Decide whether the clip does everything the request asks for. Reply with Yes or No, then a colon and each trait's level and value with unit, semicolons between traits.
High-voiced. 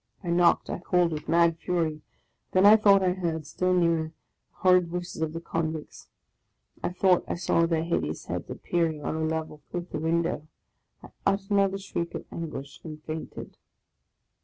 No: medium, 170 Hz